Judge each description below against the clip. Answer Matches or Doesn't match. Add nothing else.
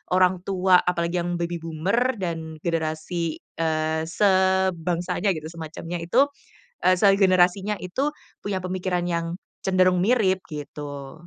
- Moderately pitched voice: Matches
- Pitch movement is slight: Matches